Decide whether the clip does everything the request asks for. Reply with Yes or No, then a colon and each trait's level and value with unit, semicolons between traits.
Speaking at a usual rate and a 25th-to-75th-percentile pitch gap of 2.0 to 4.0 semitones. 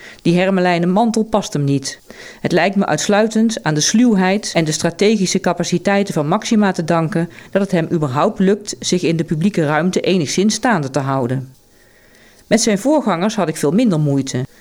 No: average, 175 wpm; average, 5.3 semitones